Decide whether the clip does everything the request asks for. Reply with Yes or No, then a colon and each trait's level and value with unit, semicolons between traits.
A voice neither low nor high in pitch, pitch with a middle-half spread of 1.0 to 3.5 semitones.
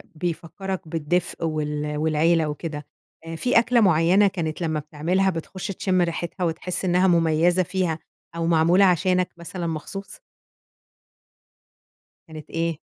Yes: medium, 170 Hz; narrow, 2.6 semitones